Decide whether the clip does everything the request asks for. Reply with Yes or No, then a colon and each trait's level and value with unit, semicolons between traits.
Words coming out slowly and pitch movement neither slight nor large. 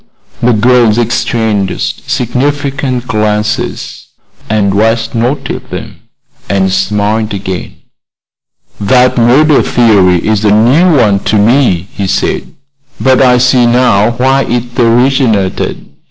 Yes: slow, 110 wpm; average, 3.3 semitones